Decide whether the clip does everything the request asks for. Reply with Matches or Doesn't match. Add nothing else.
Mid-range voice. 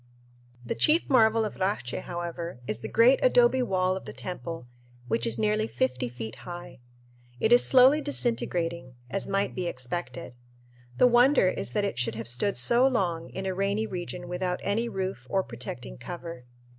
Matches